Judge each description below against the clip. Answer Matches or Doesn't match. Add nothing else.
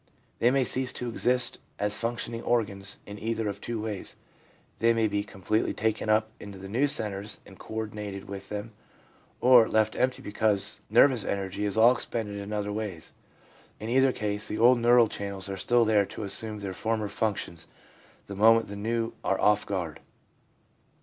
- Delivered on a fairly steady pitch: Matches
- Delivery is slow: Doesn't match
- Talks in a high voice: Doesn't match